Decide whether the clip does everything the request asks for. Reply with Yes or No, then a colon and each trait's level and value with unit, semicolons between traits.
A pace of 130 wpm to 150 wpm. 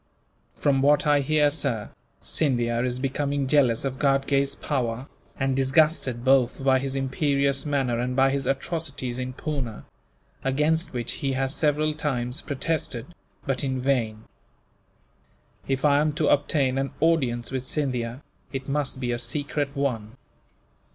Yes: average, 145 wpm